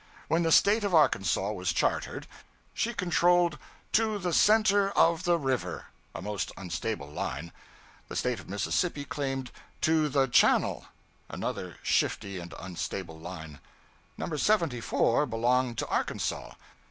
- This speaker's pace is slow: Yes, slow, 130 wpm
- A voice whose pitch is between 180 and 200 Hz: No, low, 135 Hz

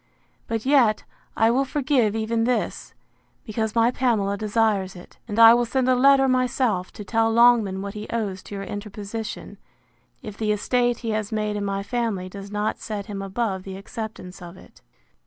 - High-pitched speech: Yes, high, 220 Hz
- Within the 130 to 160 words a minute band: No, average, 180 wpm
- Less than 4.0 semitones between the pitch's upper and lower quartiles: Yes, average, 2.9 semitones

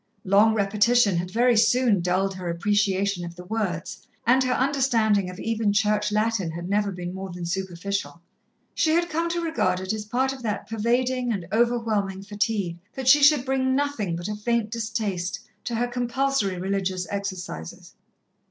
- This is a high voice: Yes, high, 210 Hz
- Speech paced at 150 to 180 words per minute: Yes, average, 170 wpm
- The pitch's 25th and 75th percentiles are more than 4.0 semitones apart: Yes, average, 4.4 semitones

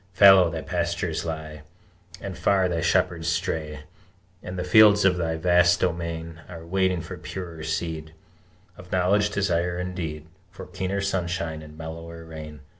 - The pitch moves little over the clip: Yes, narrow, 2.1 semitones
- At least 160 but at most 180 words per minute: No, average, 150 wpm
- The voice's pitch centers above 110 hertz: No, very low, 85 Hz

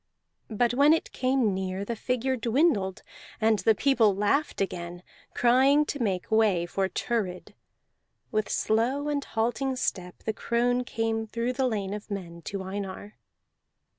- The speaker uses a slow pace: No, average, 145 wpm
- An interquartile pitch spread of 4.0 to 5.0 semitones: Yes, average, 4.3 semitones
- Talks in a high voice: Yes, high, 225 Hz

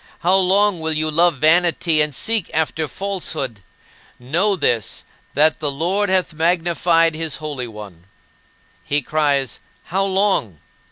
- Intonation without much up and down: No, average, 3.9 semitones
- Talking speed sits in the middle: No, slow, 130 wpm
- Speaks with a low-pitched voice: No, medium, 160 Hz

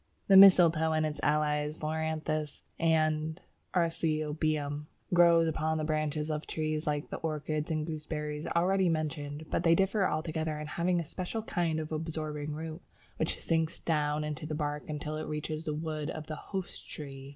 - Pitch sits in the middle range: Yes, medium, 155 Hz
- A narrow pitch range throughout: Yes, narrow, 1.3 semitones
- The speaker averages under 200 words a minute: Yes, average, 165 wpm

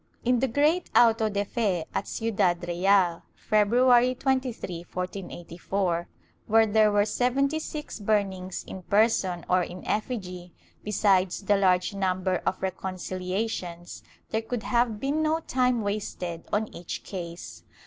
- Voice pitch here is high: Yes, high, 205 Hz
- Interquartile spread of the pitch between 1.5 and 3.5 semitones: No, average, 4.3 semitones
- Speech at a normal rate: No, slow, 130 wpm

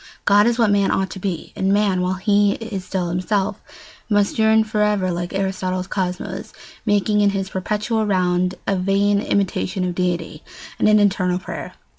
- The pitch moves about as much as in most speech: No, narrow, 2.1 semitones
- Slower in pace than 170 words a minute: No, average, 175 wpm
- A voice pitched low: No, high, 195 Hz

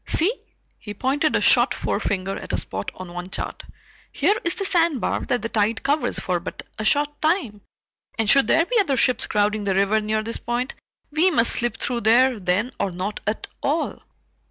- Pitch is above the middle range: Yes, high, 230 Hz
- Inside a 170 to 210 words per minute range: Yes, average, 195 wpm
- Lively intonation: Yes, wide, 5.9 semitones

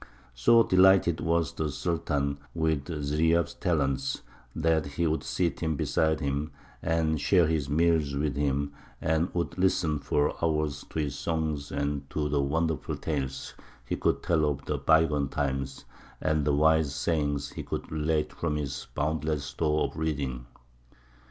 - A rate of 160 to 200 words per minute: No, average, 150 wpm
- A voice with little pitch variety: Yes, narrow, 2.3 semitones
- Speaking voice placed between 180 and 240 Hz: No, very low, 75 Hz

